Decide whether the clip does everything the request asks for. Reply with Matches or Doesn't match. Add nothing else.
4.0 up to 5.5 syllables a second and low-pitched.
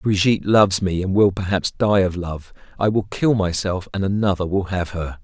Matches